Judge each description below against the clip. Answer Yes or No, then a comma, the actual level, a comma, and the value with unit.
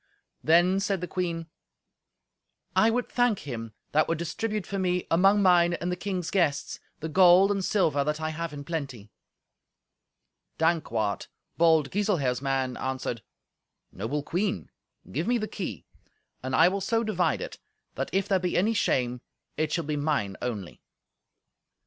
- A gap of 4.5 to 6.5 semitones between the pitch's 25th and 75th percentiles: Yes, average, 5.2 semitones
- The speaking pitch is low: No, medium, 170 Hz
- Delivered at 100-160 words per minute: Yes, average, 155 wpm